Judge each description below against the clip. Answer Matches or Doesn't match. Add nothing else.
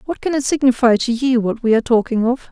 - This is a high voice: Matches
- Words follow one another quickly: Matches